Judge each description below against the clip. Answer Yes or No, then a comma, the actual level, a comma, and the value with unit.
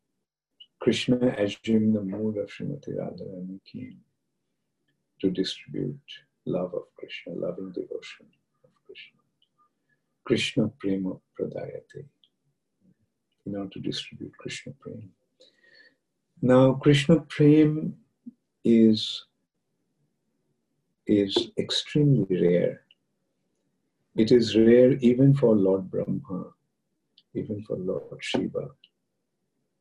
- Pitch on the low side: Yes, low, 125 Hz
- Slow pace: Yes, slow, 90 wpm